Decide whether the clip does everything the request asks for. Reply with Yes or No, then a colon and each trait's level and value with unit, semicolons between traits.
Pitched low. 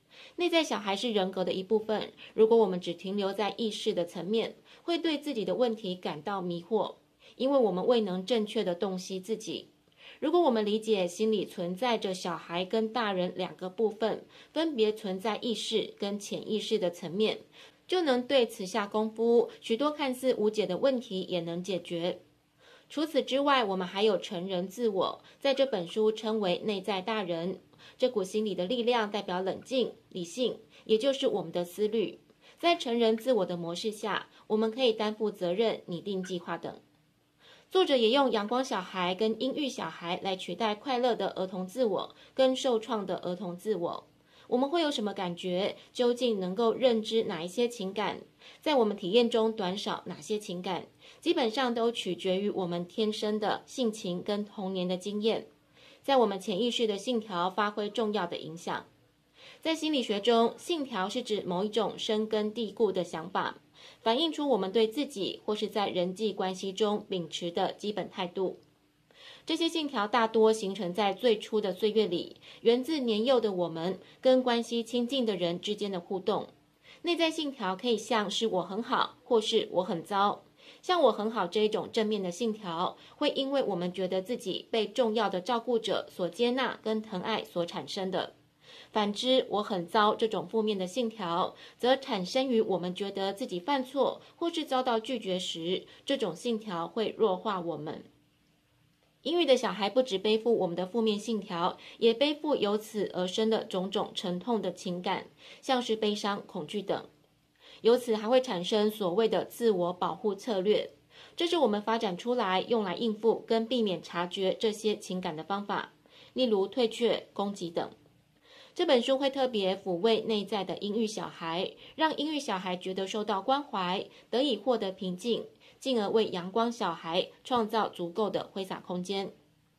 No: high, 215 Hz